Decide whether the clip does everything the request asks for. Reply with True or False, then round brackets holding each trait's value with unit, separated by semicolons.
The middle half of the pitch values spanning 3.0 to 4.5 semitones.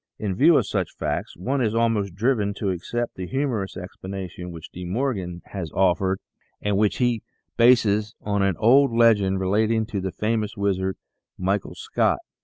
True (3.4 semitones)